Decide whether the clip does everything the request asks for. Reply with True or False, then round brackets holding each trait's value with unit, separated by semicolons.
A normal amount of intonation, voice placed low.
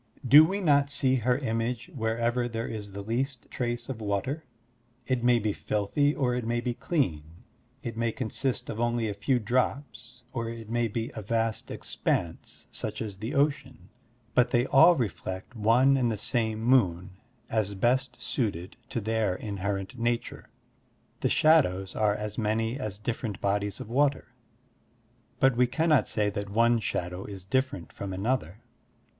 True (3.5 semitones; 115 Hz)